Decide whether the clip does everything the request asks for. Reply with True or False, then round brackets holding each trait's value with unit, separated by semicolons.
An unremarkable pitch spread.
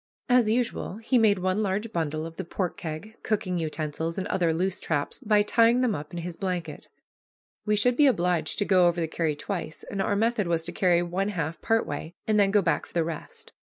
True (4.3 semitones)